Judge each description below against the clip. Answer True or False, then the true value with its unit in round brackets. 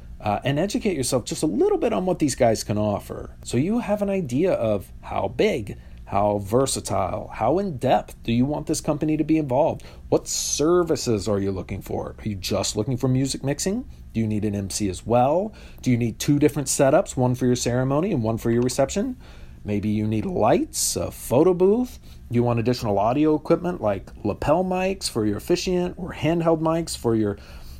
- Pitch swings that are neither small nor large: False (7.3 semitones)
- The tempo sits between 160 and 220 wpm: True (200 wpm)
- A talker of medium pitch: False (125 Hz)